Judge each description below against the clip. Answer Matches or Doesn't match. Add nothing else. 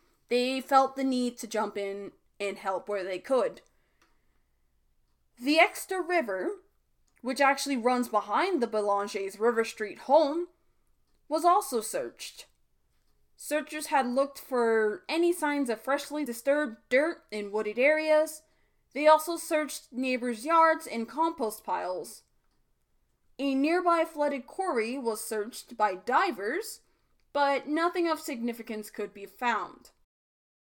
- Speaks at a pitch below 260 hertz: Doesn't match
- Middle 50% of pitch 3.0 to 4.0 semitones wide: Doesn't match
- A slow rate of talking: Matches